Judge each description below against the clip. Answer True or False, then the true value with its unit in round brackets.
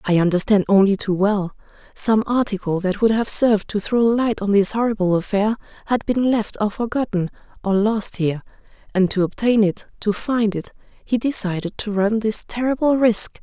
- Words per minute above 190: False (180 wpm)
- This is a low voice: False (210 Hz)